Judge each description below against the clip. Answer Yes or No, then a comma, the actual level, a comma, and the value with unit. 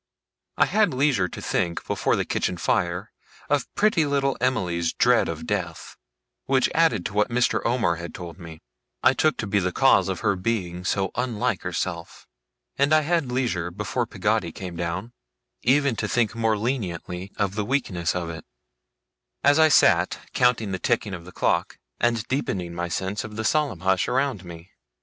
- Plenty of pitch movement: Yes, wide, 6.2 semitones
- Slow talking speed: No, average, 175 wpm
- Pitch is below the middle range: Yes, low, 105 Hz